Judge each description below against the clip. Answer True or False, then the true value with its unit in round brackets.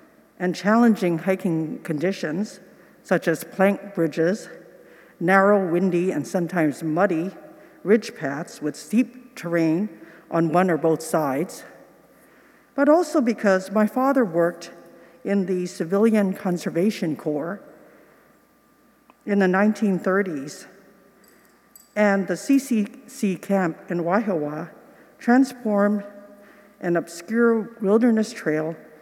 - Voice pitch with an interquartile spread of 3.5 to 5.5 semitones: True (4.9 semitones)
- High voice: True (195 Hz)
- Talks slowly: True (100 wpm)